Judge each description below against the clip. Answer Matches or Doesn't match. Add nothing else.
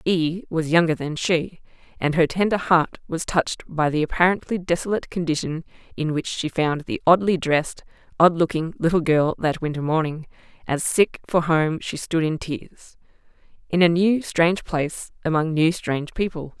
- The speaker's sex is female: Matches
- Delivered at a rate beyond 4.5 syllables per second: Matches